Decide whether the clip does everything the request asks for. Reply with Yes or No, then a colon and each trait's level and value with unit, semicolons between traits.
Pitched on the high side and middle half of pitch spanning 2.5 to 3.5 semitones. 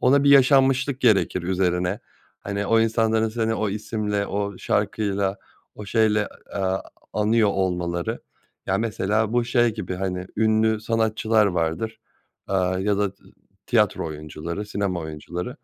No: low, 105 Hz; average, 2.9 semitones